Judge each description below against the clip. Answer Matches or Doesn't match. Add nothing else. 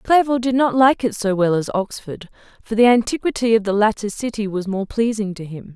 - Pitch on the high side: Matches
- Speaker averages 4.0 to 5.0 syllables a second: Doesn't match